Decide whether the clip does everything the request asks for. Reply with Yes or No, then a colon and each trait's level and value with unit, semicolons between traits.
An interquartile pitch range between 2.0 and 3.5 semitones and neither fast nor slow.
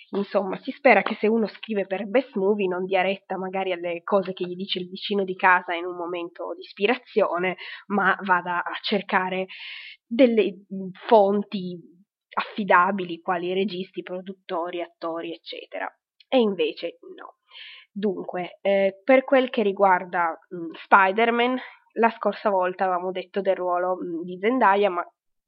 Yes: average, 2.8 semitones; average, 145 wpm